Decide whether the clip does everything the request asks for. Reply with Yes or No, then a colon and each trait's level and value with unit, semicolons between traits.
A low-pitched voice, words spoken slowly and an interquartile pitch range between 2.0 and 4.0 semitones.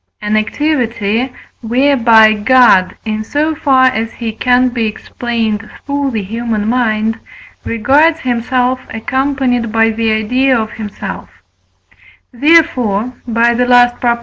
No: high, 235 Hz; slow, 120 wpm; average, 2.8 semitones